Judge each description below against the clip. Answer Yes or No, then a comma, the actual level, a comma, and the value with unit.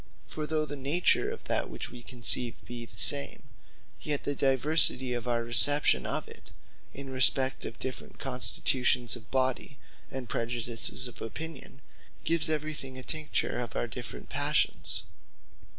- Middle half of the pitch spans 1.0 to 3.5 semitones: Yes, average, 3.1 semitones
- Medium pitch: No, low, 130 Hz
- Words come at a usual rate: Yes, average, 145 wpm